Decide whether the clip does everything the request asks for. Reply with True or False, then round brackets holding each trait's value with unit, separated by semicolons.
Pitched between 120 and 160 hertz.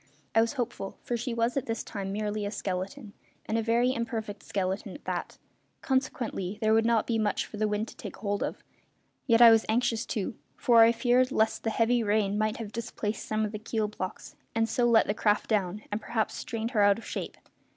False (220 Hz)